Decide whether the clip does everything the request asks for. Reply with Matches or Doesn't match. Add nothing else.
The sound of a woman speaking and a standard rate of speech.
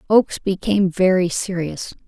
Doesn't match